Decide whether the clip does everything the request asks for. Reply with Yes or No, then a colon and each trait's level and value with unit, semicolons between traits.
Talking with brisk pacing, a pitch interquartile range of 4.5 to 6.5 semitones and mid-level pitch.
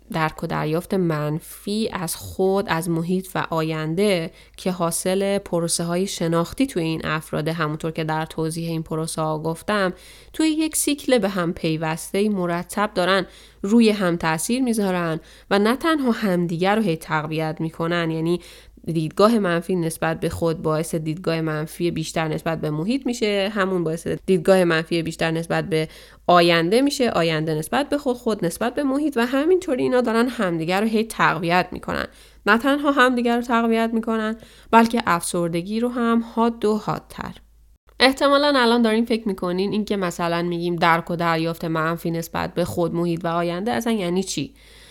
Yes: fast, 160 wpm; average, 5.3 semitones; medium, 175 Hz